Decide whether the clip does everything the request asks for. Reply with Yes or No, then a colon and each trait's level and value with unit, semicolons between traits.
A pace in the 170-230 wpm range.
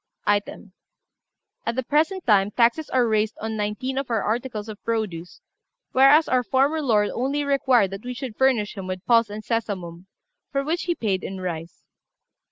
Yes: average, 175 wpm